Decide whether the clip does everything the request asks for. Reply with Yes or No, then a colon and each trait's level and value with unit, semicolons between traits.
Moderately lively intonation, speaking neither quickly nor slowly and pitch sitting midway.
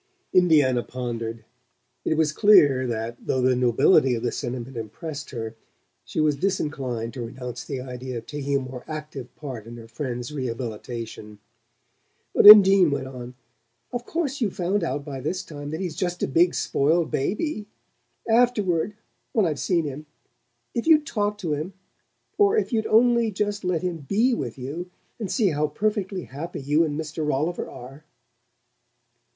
No: wide, 6.7 semitones; average, 165 wpm; medium, 150 Hz